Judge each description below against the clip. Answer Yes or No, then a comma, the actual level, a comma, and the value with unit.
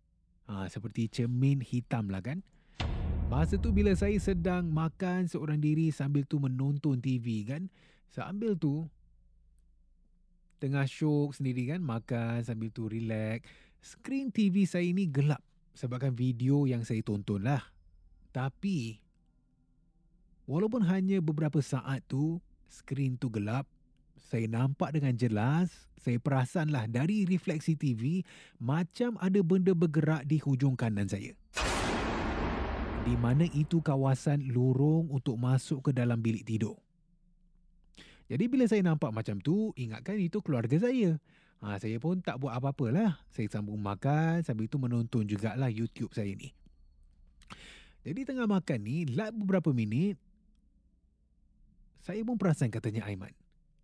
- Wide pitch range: Yes, wide, 7.0 semitones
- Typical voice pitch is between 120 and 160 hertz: Yes, medium, 140 Hz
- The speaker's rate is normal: Yes, average, 130 wpm